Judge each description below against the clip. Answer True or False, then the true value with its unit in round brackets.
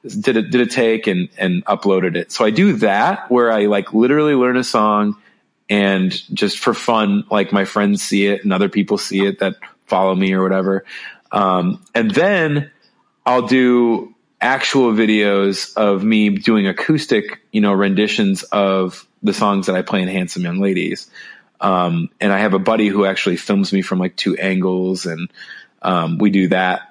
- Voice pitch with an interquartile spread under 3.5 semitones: True (2.9 semitones)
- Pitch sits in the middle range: False (100 Hz)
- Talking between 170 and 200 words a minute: True (185 wpm)